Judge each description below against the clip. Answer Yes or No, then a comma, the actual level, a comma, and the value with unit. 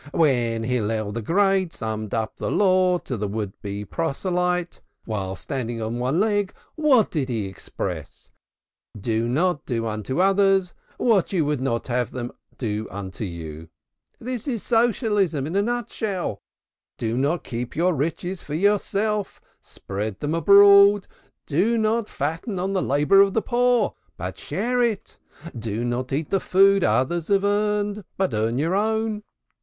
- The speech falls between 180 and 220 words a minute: No, average, 155 wpm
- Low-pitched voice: No, medium, 165 Hz